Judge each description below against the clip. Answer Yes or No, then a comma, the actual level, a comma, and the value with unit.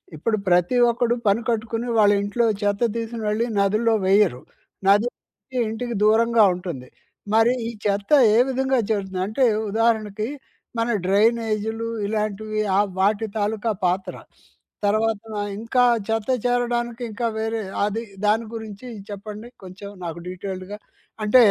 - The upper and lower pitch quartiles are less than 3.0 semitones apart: Yes, narrow, 2.4 semitones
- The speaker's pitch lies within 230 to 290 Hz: No, high, 220 Hz